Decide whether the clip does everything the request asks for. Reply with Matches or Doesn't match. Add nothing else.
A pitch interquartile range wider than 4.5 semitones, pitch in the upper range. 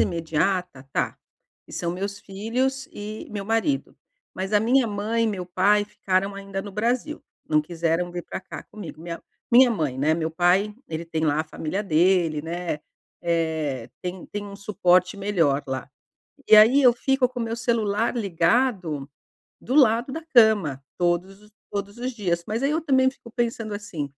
Matches